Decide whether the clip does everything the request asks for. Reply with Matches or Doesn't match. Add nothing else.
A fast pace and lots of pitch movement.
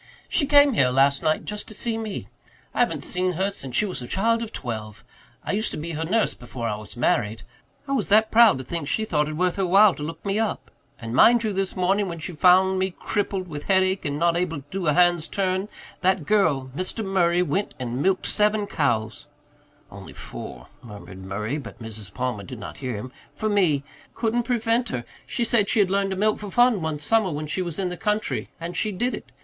Matches